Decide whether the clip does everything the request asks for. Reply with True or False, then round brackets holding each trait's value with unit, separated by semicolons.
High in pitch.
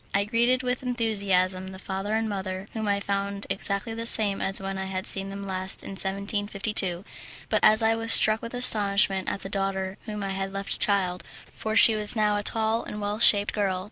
True (200 Hz)